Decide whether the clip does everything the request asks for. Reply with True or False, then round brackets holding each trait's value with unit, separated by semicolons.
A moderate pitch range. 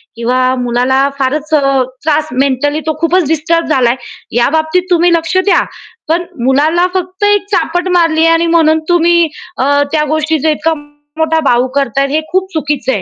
True (3.5 semitones)